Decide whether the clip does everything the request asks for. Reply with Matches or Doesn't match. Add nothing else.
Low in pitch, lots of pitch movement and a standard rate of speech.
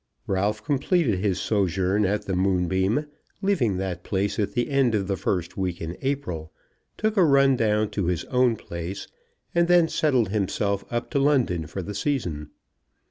Matches